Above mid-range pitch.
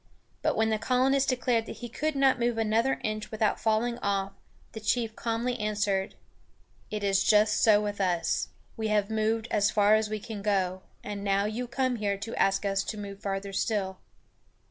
Yes: high, 215 Hz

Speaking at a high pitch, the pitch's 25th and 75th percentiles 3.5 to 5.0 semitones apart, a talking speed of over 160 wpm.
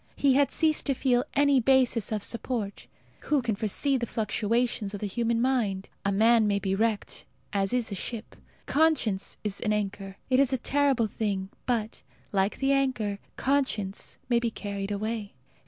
Yes: high, 230 Hz; average, 4.3 semitones; average, 170 wpm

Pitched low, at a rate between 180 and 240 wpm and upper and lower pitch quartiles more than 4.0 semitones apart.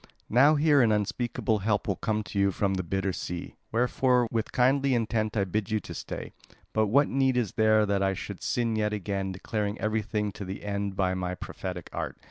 No: low, 105 Hz; average, 200 wpm; average, 3.1 semitones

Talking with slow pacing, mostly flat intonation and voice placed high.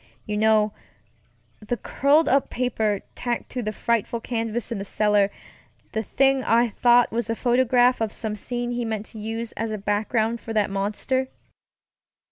No: average, 165 wpm; narrow, 2.3 semitones; high, 225 Hz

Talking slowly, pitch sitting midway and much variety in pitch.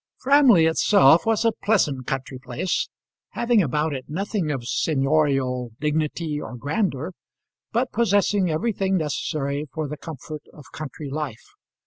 Yes: slow, 130 wpm; medium, 155 Hz; wide, 5.9 semitones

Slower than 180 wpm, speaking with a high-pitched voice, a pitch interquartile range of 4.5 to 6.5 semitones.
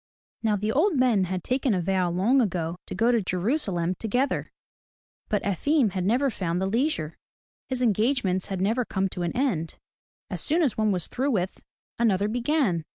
No: average, 185 wpm; high, 210 Hz; wide, 5.5 semitones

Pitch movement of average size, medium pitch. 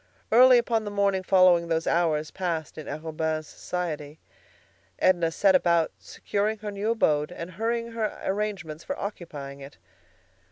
Yes: average, 4.7 semitones; medium, 180 Hz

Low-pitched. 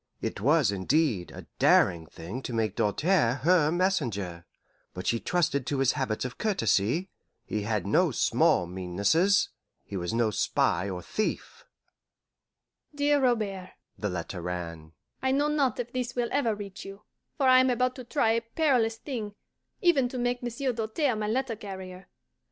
No: medium, 185 Hz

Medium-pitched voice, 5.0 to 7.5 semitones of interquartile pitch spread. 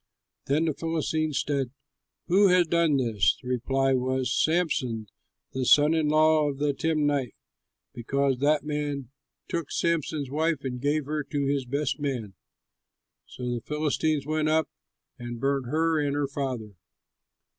No: medium, 145 Hz; average, 2.9 semitones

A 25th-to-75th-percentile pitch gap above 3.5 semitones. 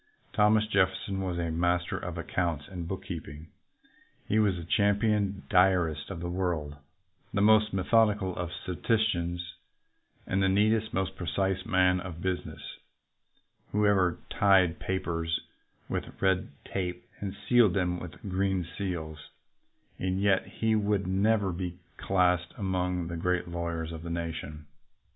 No: narrow, 2.4 semitones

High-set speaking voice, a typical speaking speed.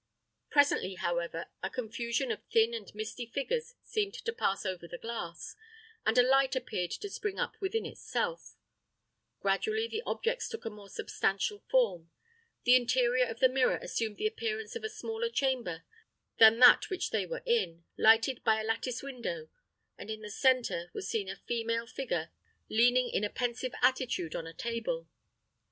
Yes: high, 240 Hz; average, 170 wpm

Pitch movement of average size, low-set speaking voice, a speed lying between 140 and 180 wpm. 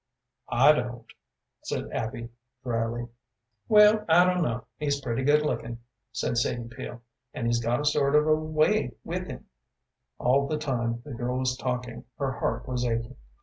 Yes: average, 4.0 semitones; low, 125 Hz; average, 165 wpm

